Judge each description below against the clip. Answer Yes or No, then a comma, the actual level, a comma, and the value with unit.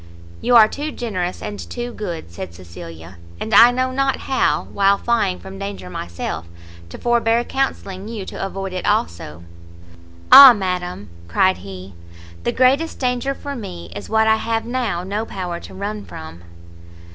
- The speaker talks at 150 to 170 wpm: Yes, average, 160 wpm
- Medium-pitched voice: No, high, 195 Hz